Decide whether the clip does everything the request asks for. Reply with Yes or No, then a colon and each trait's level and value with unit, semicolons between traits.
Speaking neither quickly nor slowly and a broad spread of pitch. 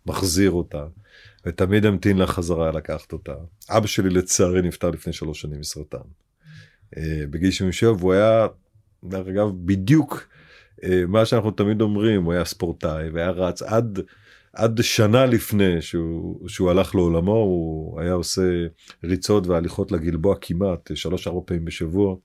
No: average, 140 wpm; average, 3.2 semitones